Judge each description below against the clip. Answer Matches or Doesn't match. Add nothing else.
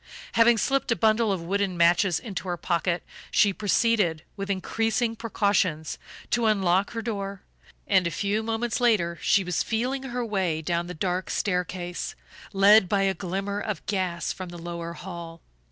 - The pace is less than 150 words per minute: Doesn't match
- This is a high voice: Matches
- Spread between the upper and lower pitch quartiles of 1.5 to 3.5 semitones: Doesn't match